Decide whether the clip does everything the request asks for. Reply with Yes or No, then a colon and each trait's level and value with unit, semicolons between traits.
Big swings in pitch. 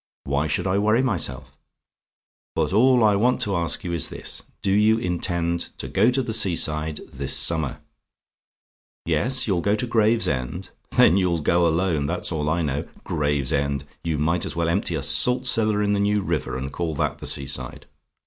Yes: wide, 5.7 semitones